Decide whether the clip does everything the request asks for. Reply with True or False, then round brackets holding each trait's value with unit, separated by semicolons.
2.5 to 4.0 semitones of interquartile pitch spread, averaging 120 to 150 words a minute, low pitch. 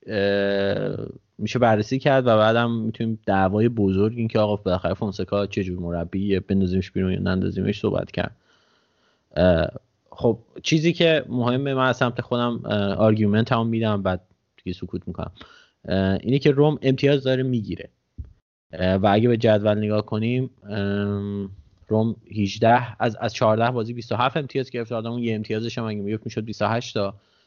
True (3.3 semitones; 145 wpm; 110 Hz)